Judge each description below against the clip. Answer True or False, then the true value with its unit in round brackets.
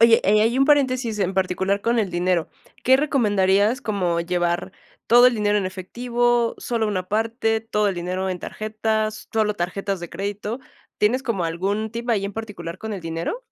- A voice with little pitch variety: False (3.7 semitones)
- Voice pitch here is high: True (210 Hz)